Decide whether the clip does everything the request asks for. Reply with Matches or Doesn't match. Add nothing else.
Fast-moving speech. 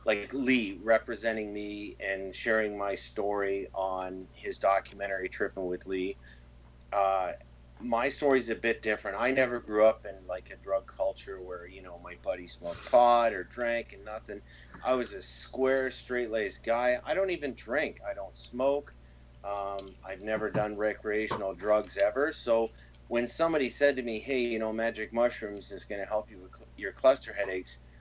Doesn't match